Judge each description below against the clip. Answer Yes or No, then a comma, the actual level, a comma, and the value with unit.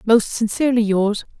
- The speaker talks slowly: Yes, slow, 130 wpm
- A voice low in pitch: No, high, 220 Hz